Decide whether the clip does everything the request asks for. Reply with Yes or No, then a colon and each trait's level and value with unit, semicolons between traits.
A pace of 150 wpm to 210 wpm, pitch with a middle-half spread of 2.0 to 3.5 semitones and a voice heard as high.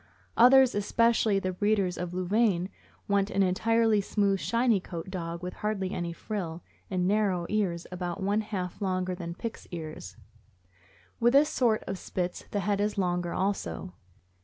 Yes: average, 155 wpm; average, 3.1 semitones; high, 195 Hz